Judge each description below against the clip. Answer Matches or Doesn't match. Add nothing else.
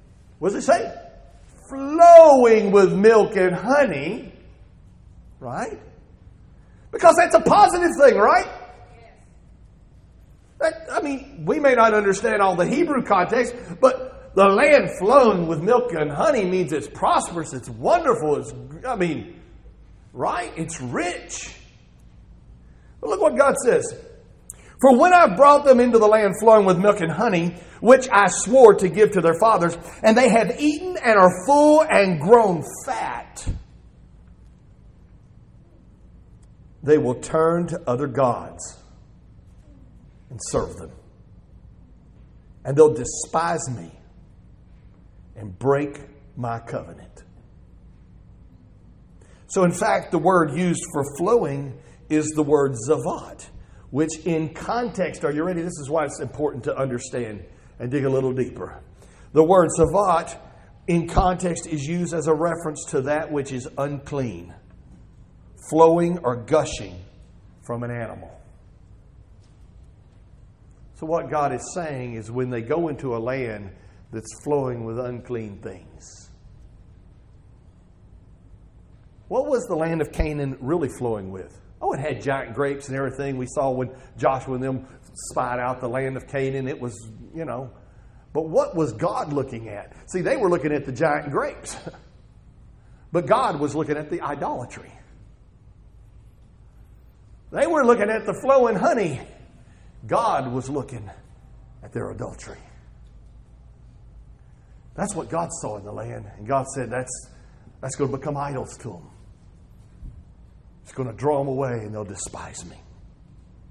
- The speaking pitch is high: Doesn't match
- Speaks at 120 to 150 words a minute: Matches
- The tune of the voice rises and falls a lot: Matches